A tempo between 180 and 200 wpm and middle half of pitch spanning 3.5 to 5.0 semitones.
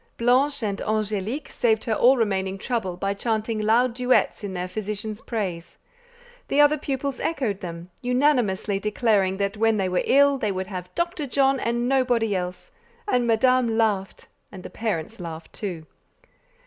No: average, 160 wpm; average, 4.5 semitones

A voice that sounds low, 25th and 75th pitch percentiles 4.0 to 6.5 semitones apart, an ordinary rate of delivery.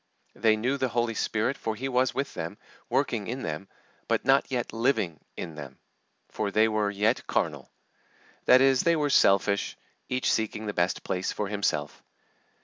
Yes: low, 110 Hz; average, 4.3 semitones; average, 170 wpm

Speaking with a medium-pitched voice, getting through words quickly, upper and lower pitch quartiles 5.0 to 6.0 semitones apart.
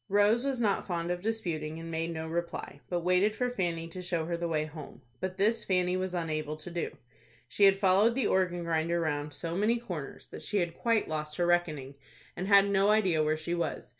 No: medium, 175 Hz; fast, 220 wpm; average, 3.6 semitones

